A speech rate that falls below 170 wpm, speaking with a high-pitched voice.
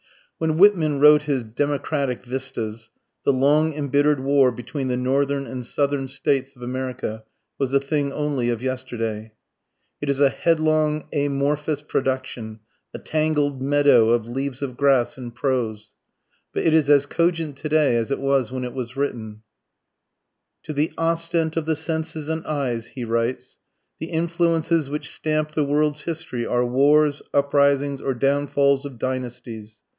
No: average, 155 wpm; medium, 140 Hz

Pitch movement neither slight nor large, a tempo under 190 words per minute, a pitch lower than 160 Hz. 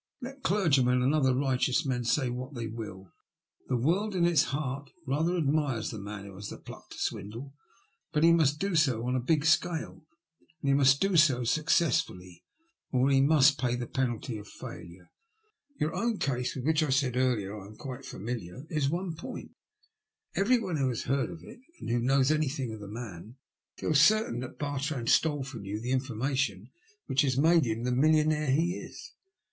No: average, 4.4 semitones; average, 195 wpm; low, 135 Hz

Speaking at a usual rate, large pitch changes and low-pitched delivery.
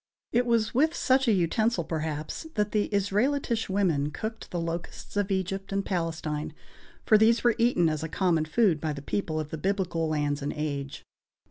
No: average, 185 wpm; wide, 5.7 semitones; medium, 185 Hz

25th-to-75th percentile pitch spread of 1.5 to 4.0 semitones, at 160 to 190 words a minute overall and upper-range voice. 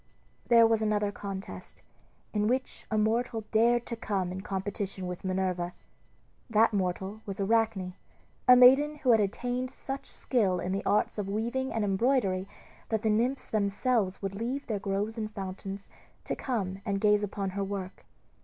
Yes: average, 3.0 semitones; average, 165 wpm; high, 210 Hz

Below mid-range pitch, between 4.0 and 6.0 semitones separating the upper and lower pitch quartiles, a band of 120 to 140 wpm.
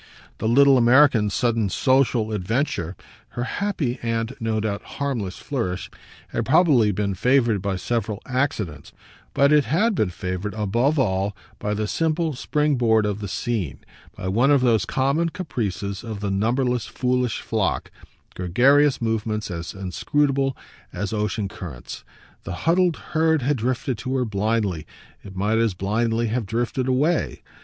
No: low, 115 Hz; average, 4.9 semitones; average, 150 wpm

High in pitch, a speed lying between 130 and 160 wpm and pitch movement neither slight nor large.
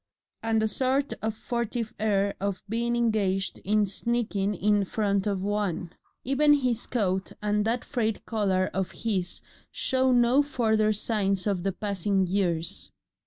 Yes: high, 210 Hz; average, 145 wpm; average, 3.3 semitones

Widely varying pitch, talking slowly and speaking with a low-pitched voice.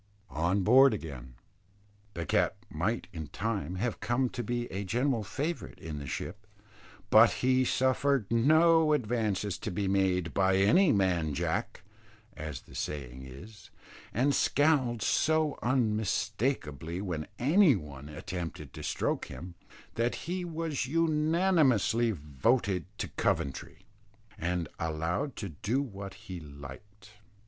Yes: wide, 7.6 semitones; slow, 130 wpm; low, 105 Hz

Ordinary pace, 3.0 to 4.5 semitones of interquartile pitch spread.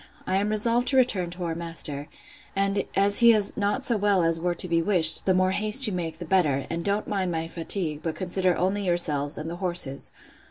No: fast, 225 wpm; average, 3.5 semitones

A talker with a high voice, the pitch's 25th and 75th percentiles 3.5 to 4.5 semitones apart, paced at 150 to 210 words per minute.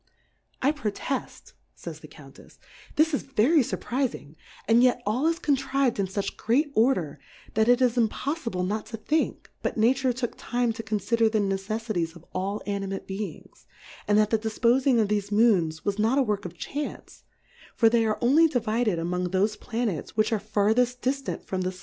Yes: high, 225 Hz; average, 3.8 semitones; average, 180 wpm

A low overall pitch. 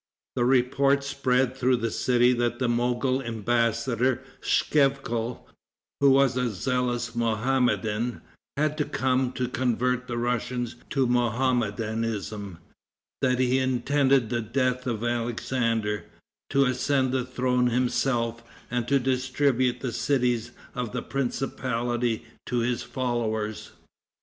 Yes: low, 125 Hz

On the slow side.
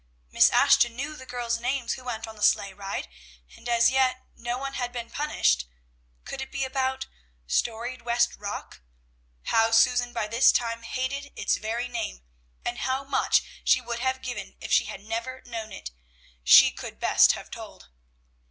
No: average, 175 wpm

